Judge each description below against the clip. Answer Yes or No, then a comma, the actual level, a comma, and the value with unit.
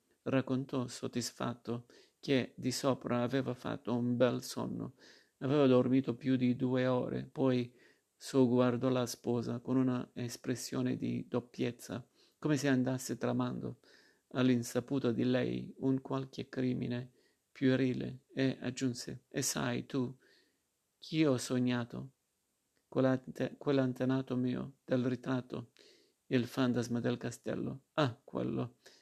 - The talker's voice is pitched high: No, low, 125 Hz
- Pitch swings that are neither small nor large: No, narrow, 1.4 semitones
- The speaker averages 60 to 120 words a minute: Yes, slow, 115 wpm